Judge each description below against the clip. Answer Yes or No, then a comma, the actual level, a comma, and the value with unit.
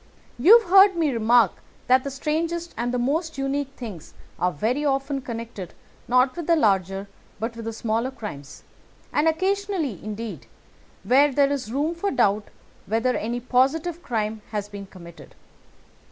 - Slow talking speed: No, average, 155 wpm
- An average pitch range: No, wide, 5.8 semitones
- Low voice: No, very high, 255 Hz